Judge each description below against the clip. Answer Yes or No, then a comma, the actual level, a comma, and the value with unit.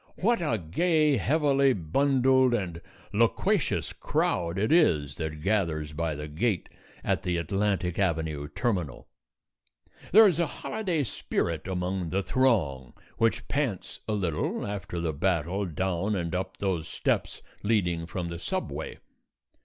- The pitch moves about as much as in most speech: No, wide, 6.6 semitones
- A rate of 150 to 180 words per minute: No, slow, 135 wpm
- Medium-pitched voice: No, very low, 95 Hz